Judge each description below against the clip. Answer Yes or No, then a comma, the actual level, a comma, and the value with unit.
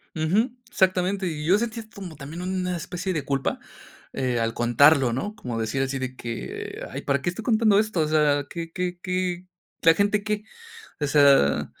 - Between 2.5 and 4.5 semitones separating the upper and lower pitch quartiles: No, wide, 5.4 semitones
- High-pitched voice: No, medium, 165 Hz